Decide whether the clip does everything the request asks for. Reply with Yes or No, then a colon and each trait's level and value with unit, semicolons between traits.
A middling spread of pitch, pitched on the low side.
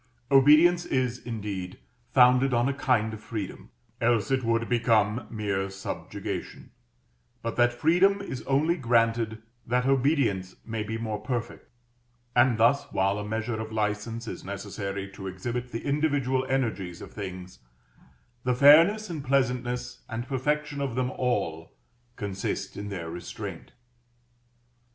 Yes: average, 4.0 semitones; low, 120 Hz